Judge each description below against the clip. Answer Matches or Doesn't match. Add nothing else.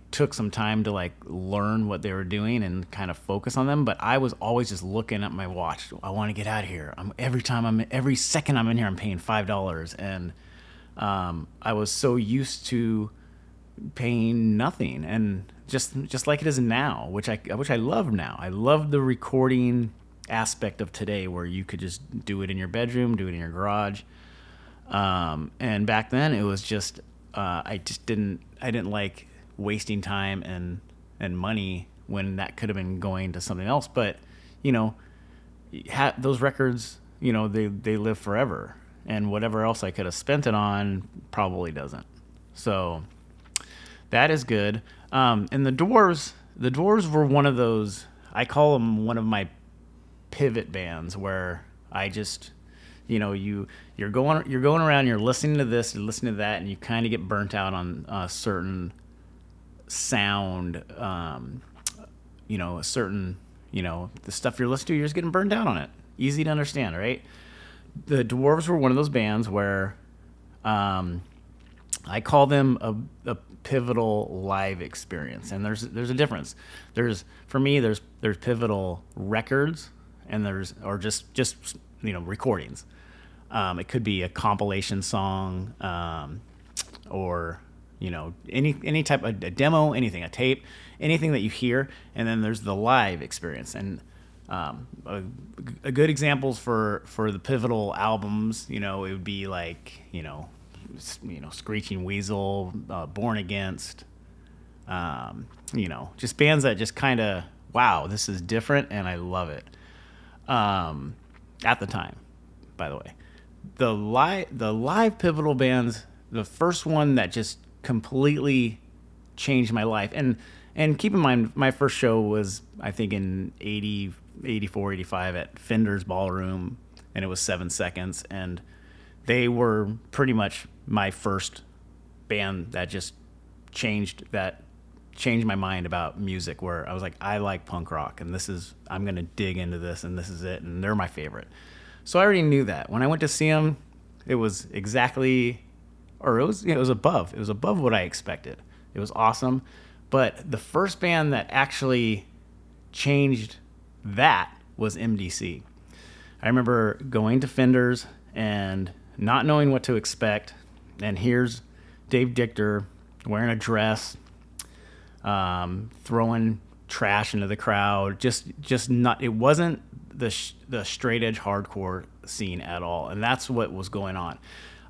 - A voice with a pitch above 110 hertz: Doesn't match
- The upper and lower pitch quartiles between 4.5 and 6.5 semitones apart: Matches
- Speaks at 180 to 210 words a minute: Doesn't match